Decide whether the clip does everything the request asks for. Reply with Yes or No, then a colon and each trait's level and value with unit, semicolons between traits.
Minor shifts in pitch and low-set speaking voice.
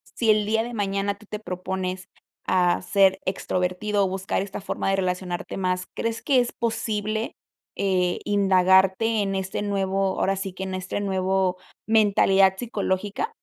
No: narrow, 1.9 semitones; high, 195 Hz